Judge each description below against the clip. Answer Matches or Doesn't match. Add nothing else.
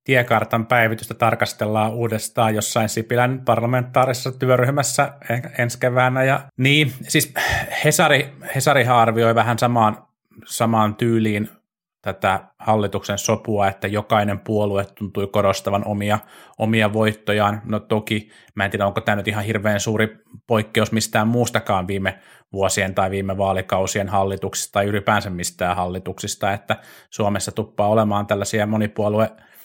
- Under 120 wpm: Doesn't match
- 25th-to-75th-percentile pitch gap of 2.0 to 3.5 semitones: Matches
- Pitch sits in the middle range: Doesn't match